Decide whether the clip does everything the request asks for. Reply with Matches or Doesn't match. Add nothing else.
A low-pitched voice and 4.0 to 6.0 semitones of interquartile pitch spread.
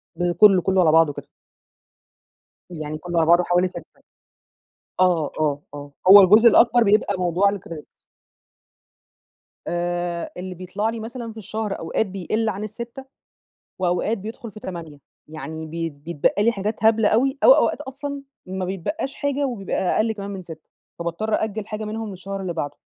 Doesn't match